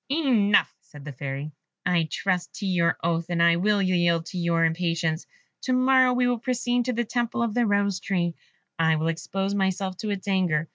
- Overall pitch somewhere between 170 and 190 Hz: Yes, medium, 185 Hz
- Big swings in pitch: No, average, 4.9 semitones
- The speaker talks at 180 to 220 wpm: Yes, average, 195 wpm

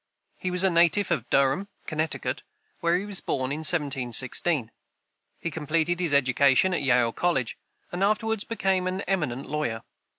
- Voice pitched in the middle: Yes, medium, 160 Hz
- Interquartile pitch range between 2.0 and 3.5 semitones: No, average, 5.2 semitones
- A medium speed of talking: Yes, average, 155 wpm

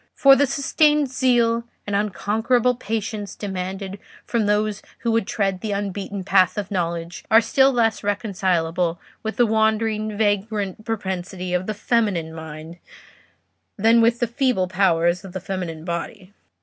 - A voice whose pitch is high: Yes, high, 205 Hz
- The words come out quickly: No, average, 145 wpm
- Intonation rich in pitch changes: No, average, 3.6 semitones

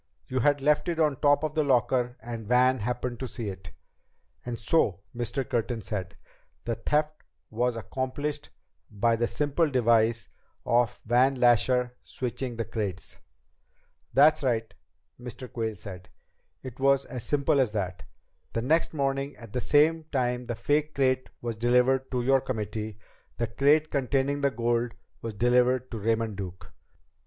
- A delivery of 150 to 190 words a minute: Yes, average, 155 wpm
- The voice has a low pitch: Yes, low, 125 Hz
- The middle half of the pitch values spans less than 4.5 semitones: Yes, average, 3.1 semitones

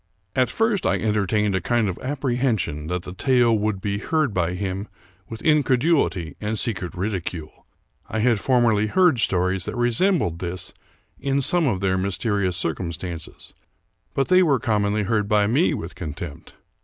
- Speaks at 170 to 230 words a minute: No, average, 155 wpm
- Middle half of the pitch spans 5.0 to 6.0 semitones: Yes, average, 5.3 semitones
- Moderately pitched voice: No, low, 105 Hz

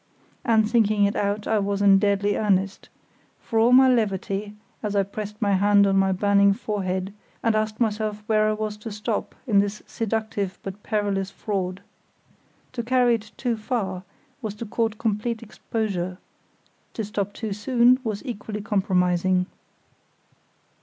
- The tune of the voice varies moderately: No, narrow, 1.9 semitones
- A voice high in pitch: Yes, high, 210 Hz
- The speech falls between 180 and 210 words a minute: No, average, 155 wpm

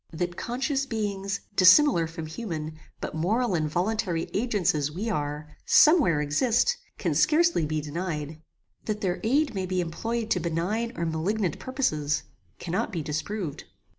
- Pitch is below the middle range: No, medium, 185 Hz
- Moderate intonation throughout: No, wide, 6.0 semitones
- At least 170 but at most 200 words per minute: No, average, 150 wpm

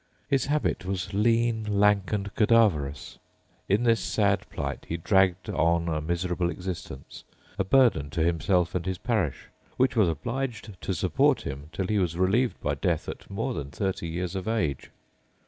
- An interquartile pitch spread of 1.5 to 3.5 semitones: No, average, 4.7 semitones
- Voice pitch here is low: Yes, very low, 95 Hz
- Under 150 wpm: No, average, 165 wpm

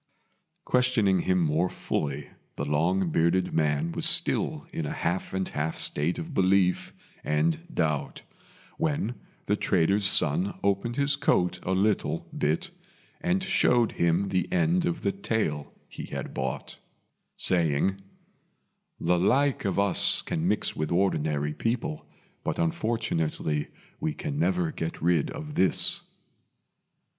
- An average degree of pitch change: No, wide, 6.8 semitones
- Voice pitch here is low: Yes, very low, 95 Hz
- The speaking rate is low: Yes, slow, 130 wpm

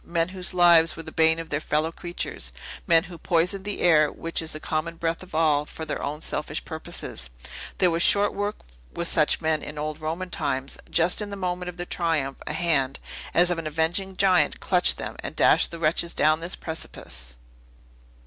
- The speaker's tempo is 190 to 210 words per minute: Yes, average, 200 wpm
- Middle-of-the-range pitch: Yes, medium, 165 Hz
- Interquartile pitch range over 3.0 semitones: No, narrow, 2.4 semitones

